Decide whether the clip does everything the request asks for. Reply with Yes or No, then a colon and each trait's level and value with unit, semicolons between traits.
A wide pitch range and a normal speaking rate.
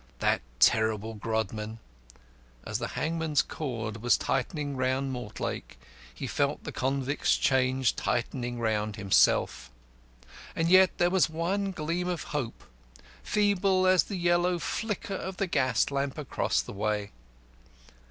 No: wide, 7.5 semitones; slow, 130 wpm